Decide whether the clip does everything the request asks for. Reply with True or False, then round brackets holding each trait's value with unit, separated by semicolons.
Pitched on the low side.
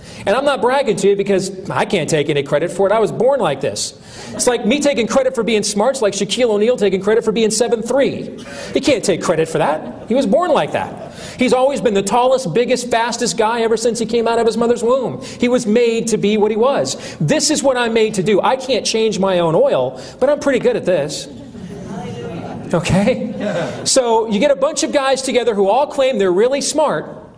False (230 Hz)